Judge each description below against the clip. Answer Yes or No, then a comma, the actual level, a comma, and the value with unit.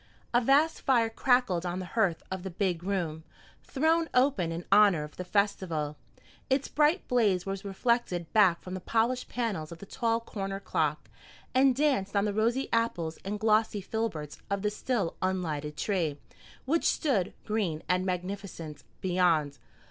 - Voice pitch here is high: Yes, high, 195 Hz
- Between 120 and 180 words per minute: Yes, average, 160 wpm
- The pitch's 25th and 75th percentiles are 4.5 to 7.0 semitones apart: Yes, average, 4.8 semitones